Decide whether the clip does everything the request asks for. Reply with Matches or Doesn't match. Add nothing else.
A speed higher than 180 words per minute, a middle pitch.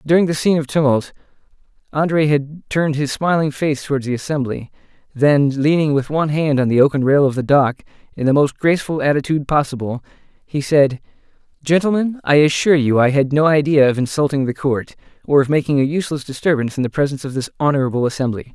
Matches